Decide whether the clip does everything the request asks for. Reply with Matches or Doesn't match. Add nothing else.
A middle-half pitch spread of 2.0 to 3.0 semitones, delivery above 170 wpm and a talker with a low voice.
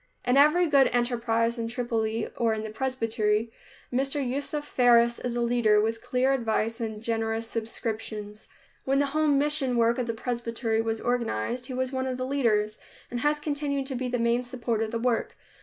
Doesn't match